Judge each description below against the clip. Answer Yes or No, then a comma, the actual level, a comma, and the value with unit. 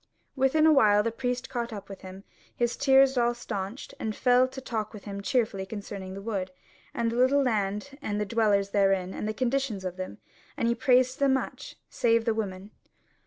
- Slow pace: No, average, 200 wpm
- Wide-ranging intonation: No, average, 4.2 semitones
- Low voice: No, high, 225 Hz